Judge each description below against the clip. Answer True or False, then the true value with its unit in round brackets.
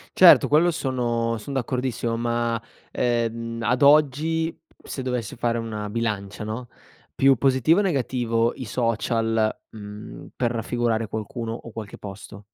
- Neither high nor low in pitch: False (115 Hz)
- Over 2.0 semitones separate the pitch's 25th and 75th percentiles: True (2.4 semitones)